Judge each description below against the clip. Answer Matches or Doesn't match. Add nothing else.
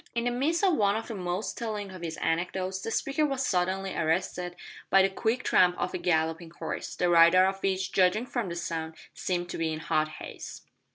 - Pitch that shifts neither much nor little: Matches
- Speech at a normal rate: Doesn't match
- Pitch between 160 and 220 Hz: Matches